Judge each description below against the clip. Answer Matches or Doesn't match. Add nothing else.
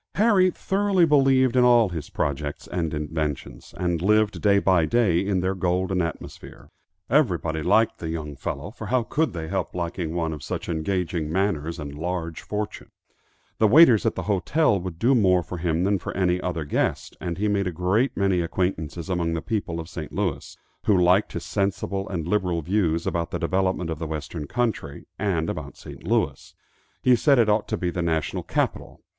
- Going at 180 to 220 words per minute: Matches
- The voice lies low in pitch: Matches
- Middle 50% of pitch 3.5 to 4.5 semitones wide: Matches